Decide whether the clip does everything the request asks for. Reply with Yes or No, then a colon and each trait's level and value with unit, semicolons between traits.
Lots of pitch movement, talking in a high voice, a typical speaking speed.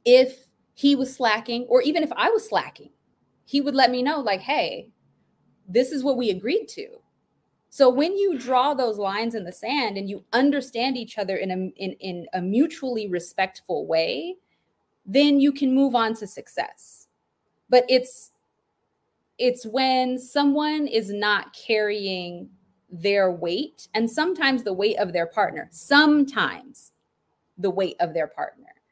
Yes: wide, 5.9 semitones; very high, 250 Hz; average, 155 wpm